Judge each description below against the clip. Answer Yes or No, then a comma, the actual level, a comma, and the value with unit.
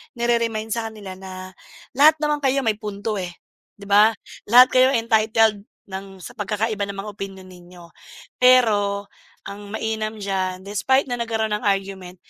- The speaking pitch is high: Yes, high, 210 Hz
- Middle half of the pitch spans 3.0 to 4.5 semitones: No, narrow, 2.6 semitones